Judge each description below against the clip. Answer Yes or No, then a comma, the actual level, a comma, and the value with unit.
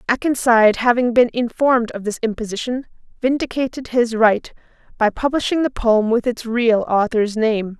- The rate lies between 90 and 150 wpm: Yes, average, 145 wpm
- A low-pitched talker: No, high, 235 Hz